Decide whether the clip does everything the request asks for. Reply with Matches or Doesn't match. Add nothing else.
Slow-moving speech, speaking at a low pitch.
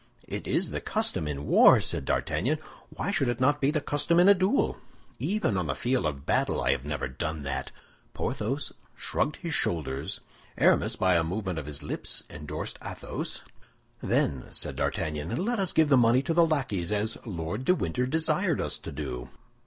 Doesn't match